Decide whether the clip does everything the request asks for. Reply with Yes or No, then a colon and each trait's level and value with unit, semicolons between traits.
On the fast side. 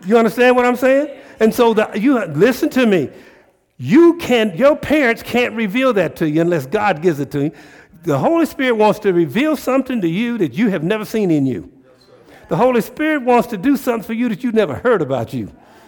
Yes: fast, 220 wpm